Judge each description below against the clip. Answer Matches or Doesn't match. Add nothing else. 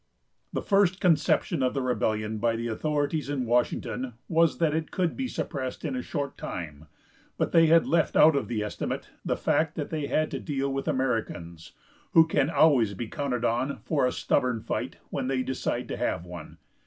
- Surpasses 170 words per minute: Matches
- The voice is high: Doesn't match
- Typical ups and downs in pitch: Matches